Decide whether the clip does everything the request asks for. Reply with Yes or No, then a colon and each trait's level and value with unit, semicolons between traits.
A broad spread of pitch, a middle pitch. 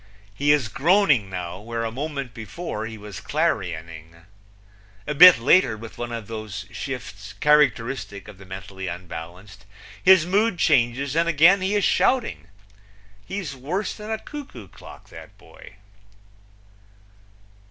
No: wide, 8.2 semitones; low, 115 Hz